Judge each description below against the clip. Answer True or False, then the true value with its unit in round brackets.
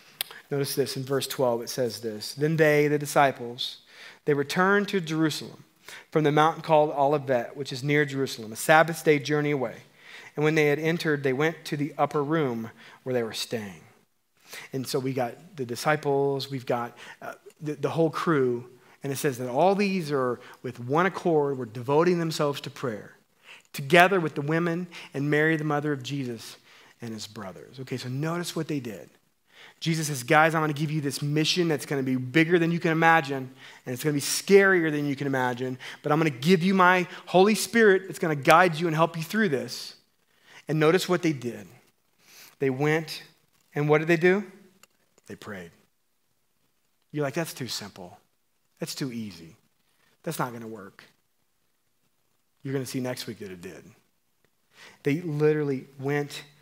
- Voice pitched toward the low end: False (150 Hz)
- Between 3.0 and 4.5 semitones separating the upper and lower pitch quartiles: True (3.5 semitones)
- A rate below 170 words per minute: False (190 wpm)